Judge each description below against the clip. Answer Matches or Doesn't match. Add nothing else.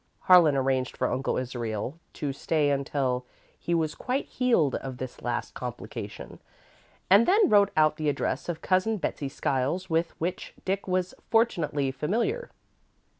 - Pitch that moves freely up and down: Matches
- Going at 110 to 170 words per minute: Matches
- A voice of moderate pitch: Matches